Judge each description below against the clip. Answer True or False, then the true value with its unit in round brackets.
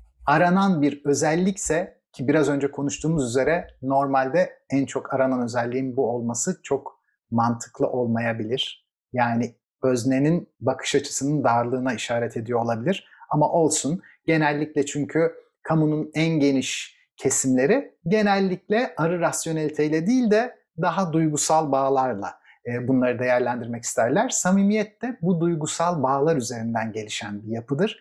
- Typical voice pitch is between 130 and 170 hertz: True (140 Hz)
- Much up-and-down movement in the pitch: False (4.9 semitones)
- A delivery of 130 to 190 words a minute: False (115 wpm)